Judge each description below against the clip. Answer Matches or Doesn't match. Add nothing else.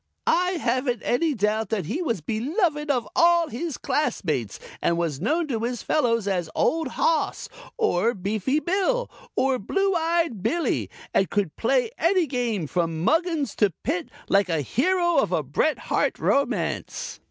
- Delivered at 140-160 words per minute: Matches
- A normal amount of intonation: Doesn't match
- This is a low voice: Doesn't match